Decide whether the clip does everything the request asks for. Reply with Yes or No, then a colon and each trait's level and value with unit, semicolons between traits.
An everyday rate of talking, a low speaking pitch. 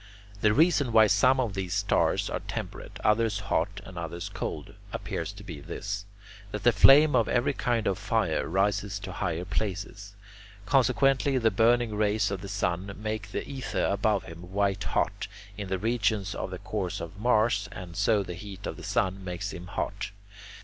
Yes: average, 180 wpm; low, 100 Hz